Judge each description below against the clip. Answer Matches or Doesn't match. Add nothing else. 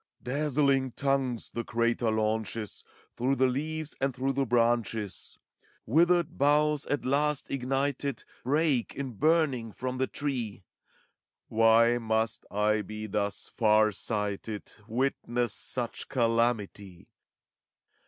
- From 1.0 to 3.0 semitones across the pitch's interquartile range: Doesn't match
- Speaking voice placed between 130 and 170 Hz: Doesn't match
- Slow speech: Matches